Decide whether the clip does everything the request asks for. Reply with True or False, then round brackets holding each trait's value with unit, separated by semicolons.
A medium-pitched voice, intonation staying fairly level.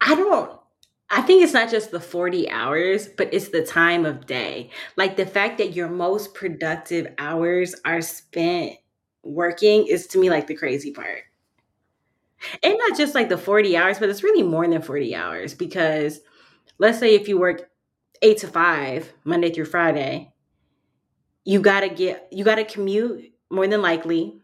False (180 Hz; 4.1 semitones)